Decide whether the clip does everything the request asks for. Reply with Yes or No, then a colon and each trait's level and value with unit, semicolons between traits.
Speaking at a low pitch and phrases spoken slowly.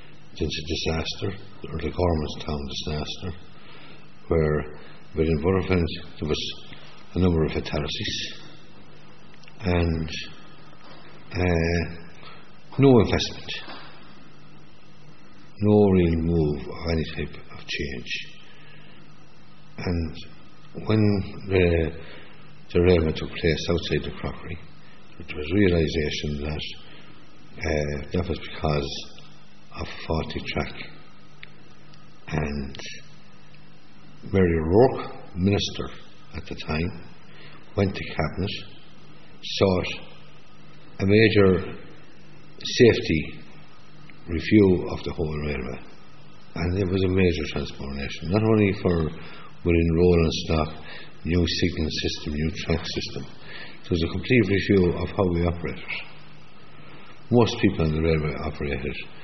Yes: very low, 85 Hz; slow, 100 wpm